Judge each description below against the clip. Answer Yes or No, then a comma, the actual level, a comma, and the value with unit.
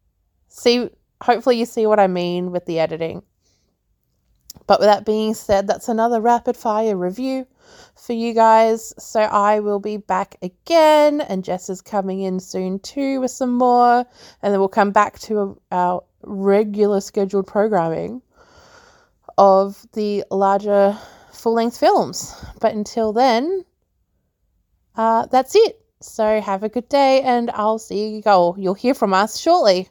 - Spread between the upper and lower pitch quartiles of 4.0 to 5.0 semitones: No, average, 3.6 semitones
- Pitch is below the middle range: No, high, 215 Hz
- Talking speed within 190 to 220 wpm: No, average, 155 wpm